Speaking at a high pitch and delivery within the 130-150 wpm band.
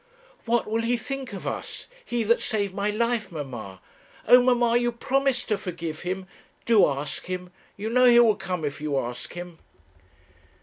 No: high, 210 Hz; average, 175 wpm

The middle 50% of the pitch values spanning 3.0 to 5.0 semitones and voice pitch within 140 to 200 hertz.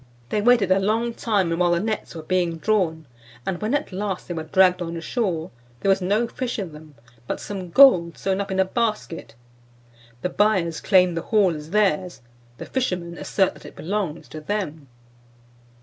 Yes: average, 3.9 semitones; medium, 185 Hz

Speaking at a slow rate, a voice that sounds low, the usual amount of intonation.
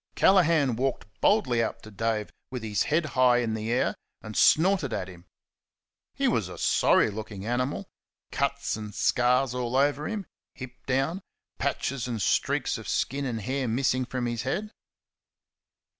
No: average, 160 wpm; low, 125 Hz; average, 3.6 semitones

